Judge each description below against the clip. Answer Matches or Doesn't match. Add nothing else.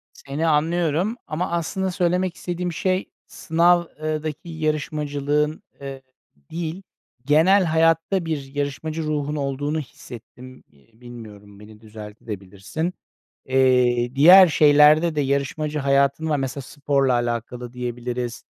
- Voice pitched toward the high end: Doesn't match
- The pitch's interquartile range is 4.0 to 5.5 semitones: Matches